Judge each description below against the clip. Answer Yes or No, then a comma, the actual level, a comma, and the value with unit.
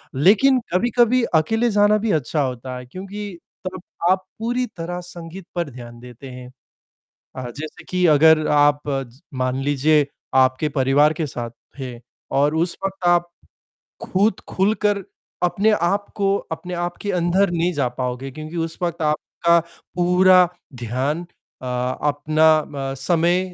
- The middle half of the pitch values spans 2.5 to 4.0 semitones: No, wide, 5.4 semitones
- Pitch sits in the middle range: Yes, medium, 165 Hz